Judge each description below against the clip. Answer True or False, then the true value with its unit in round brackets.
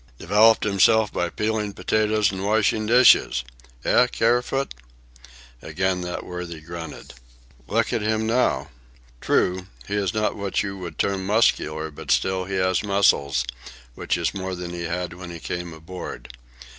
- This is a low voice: True (95 Hz)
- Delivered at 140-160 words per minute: True (150 wpm)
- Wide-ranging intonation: False (3.7 semitones)